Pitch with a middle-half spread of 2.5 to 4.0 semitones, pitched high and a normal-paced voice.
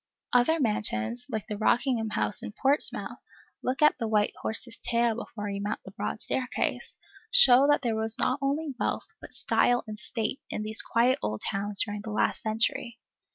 Yes: average, 3.1 semitones; high, 230 Hz; average, 180 wpm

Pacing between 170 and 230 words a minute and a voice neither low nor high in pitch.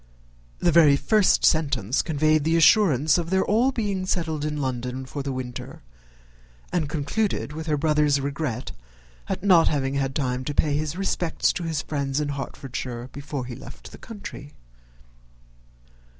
No: average, 155 wpm; medium, 150 Hz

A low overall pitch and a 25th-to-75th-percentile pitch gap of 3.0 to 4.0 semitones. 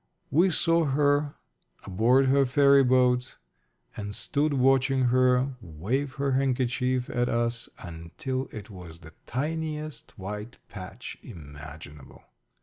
No: low, 125 Hz; average, 5.1 semitones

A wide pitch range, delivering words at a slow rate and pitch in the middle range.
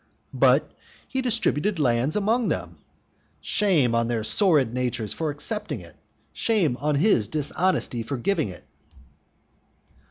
Yes: wide, 9.0 semitones; slow, 125 wpm; medium, 150 Hz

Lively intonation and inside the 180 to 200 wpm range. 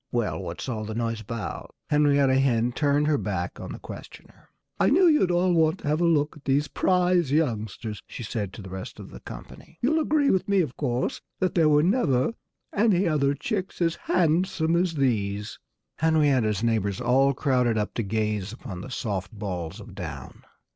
Yes: wide, 7.3 semitones; average, 190 wpm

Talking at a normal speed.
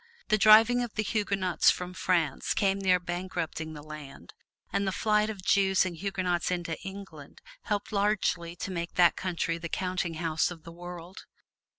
Yes: average, 170 wpm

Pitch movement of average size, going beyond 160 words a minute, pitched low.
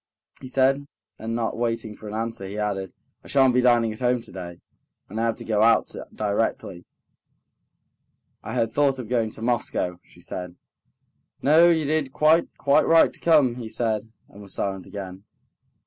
Yes: average, 4.0 semitones; average, 180 wpm; low, 115 Hz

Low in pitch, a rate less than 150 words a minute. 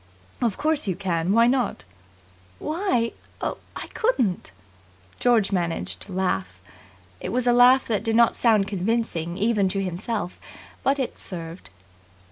No: high, 215 Hz; average, 140 wpm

